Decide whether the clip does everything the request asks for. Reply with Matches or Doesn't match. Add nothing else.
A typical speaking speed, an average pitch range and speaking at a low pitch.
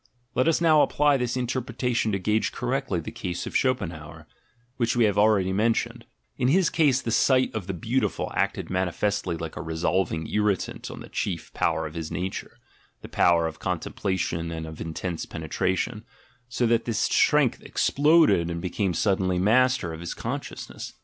Doesn't match